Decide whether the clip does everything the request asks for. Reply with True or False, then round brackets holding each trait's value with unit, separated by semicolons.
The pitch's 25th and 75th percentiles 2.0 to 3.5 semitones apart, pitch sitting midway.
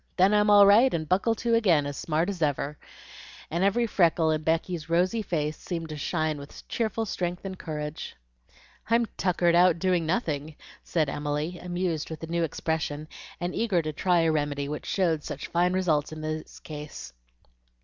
True (3.2 semitones; 165 Hz)